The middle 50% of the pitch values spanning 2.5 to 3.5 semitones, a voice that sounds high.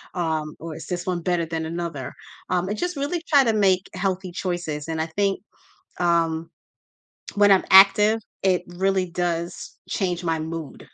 No: average, 2.8 semitones; medium, 175 Hz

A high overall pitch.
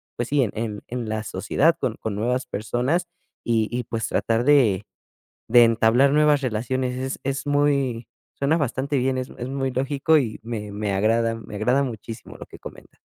No: low, 125 Hz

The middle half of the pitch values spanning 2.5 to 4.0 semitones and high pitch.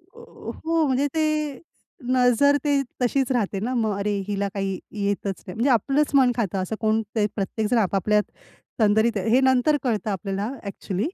No: average, 4.5 semitones; high, 220 Hz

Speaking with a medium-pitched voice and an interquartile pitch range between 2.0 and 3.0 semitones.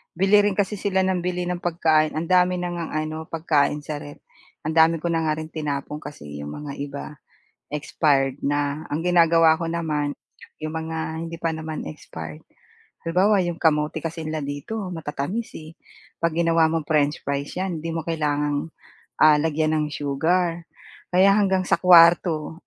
Yes: medium, 160 Hz; average, 2.7 semitones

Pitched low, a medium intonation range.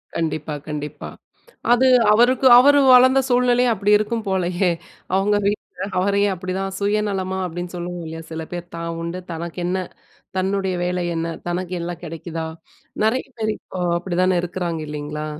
No: medium, 185 Hz; average, 3.5 semitones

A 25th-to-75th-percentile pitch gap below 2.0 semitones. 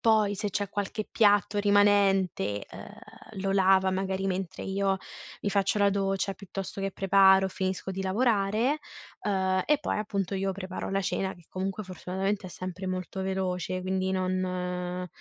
Yes: narrow, 1.2 semitones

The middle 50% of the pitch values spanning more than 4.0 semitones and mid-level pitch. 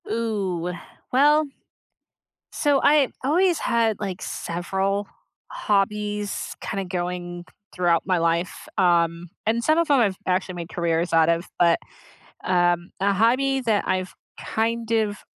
No: average, 4.7 semitones; high, 195 Hz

